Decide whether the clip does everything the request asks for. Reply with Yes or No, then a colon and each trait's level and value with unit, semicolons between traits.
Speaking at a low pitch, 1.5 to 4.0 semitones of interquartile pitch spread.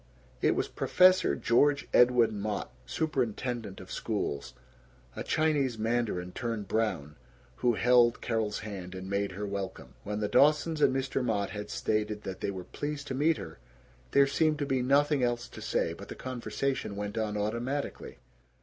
No: low, 115 Hz; average, 4.9 semitones